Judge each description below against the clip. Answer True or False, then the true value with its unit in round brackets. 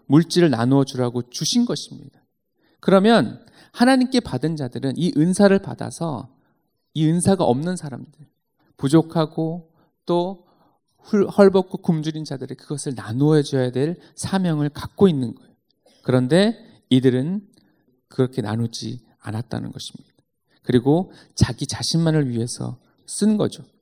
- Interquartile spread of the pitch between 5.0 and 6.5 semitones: True (5.5 semitones)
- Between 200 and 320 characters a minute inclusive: True (280 characters per minute)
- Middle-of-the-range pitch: True (155 Hz)